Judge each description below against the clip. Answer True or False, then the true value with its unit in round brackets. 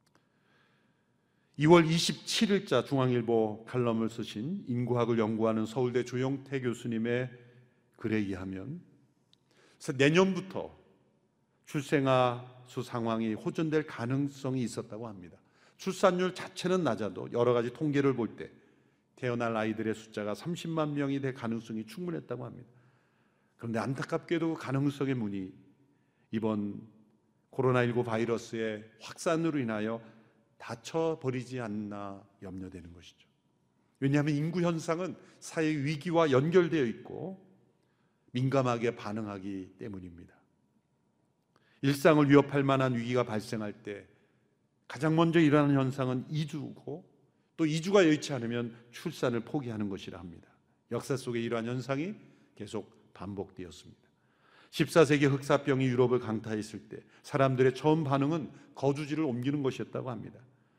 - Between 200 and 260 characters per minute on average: False (285 characters per minute)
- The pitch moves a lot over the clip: False (5.0 semitones)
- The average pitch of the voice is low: True (125 Hz)